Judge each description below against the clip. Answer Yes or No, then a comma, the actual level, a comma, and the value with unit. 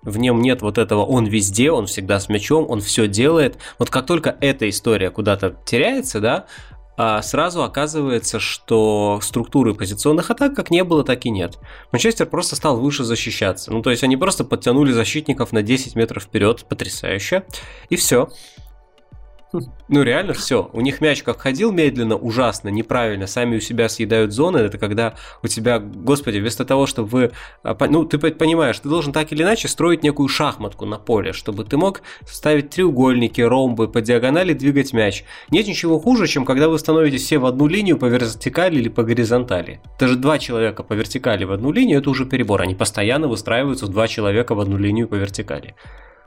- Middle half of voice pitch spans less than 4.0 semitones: No, average, 4.8 semitones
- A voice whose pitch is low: Yes, low, 120 Hz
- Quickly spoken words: Yes, fast, 180 wpm